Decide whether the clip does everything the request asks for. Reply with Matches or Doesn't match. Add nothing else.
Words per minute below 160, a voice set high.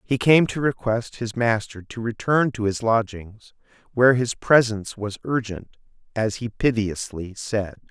Doesn't match